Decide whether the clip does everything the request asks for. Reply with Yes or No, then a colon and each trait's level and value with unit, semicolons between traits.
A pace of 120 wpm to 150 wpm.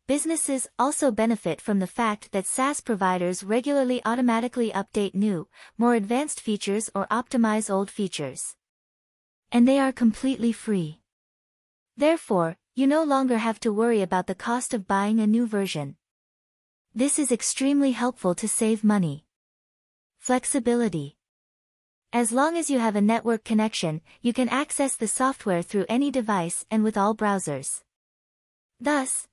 Yes: average, 140 wpm